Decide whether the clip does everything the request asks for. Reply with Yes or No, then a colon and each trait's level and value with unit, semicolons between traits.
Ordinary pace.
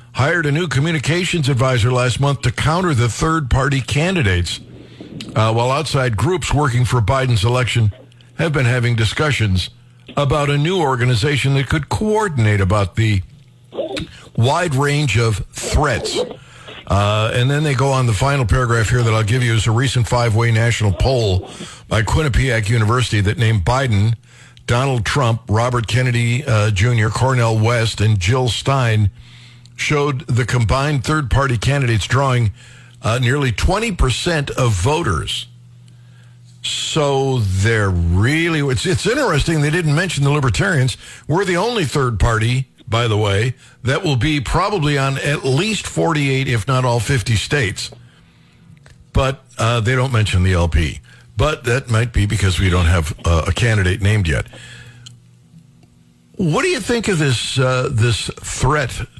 Yes: average, 150 wpm